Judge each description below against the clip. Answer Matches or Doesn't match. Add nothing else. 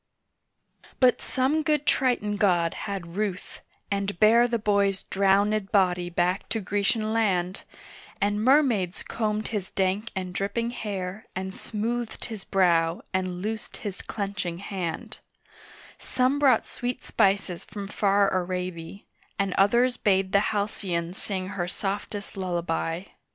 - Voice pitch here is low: Doesn't match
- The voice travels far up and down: Doesn't match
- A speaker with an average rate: Doesn't match